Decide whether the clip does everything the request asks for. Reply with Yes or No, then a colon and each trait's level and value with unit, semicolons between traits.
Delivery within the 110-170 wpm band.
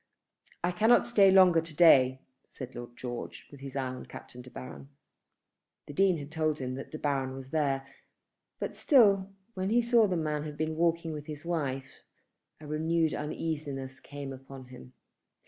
No: average, 180 wpm